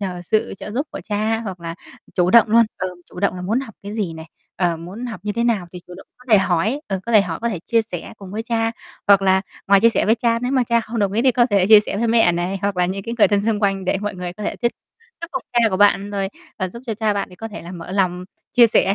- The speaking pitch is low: No, high, 205 Hz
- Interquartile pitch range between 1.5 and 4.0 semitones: Yes, average, 3.5 semitones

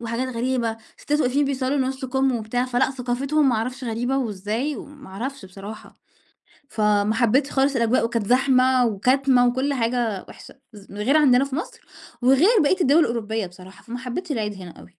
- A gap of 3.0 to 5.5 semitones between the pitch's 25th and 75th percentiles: Yes, average, 3.4 semitones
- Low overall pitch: No, very high, 250 Hz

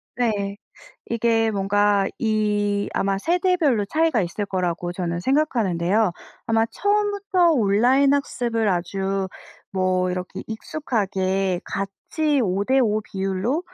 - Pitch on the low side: No, high, 210 Hz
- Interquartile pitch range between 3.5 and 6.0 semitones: Yes, average, 5.2 semitones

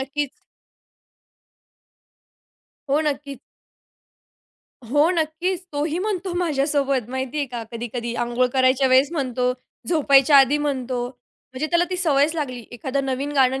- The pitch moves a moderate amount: Yes, average, 3.0 semitones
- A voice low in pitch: No, very high, 275 Hz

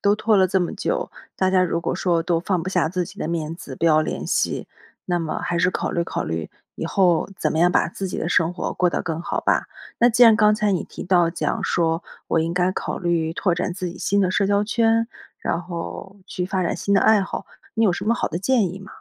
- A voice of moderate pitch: Yes, medium, 180 Hz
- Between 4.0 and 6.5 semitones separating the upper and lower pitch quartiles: No, average, 2.7 semitones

